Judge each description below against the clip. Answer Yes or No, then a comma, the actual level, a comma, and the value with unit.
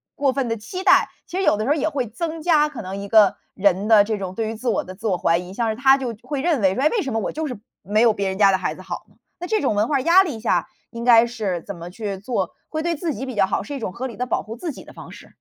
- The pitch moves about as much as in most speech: No, wide, 5.9 semitones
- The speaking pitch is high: Yes, high, 230 Hz